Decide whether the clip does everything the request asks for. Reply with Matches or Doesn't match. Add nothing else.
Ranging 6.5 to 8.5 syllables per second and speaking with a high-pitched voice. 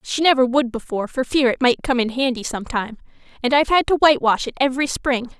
Matches